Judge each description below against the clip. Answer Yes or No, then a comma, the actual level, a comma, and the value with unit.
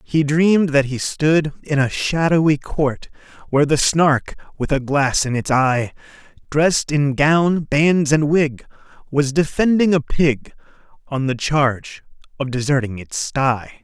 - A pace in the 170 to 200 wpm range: No, average, 150 wpm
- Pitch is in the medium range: Yes, medium, 145 Hz